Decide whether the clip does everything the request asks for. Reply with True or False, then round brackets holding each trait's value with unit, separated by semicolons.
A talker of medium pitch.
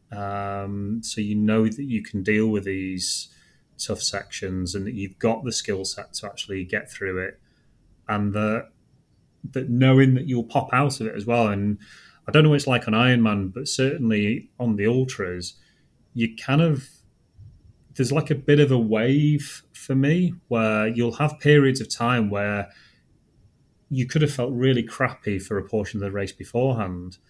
False (115 Hz)